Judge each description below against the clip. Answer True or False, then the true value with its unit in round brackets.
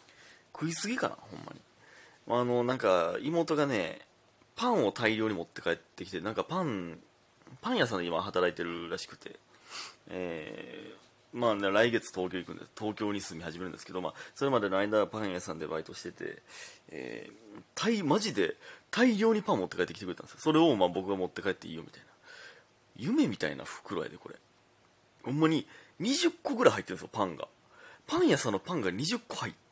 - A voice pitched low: True (110 Hz)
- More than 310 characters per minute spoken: True (380 characters per minute)